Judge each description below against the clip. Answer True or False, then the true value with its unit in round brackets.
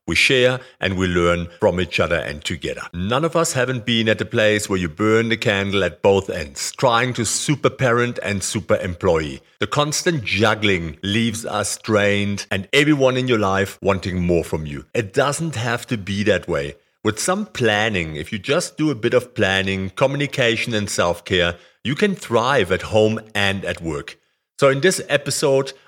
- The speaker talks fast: False (190 wpm)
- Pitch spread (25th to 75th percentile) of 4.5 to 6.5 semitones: True (5.1 semitones)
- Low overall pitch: True (110 Hz)